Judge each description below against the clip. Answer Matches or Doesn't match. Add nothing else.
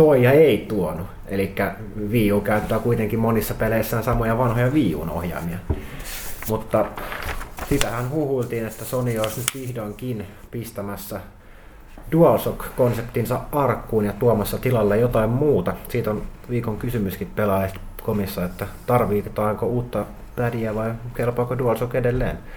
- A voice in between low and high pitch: Doesn't match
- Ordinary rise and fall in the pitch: Matches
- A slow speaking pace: Doesn't match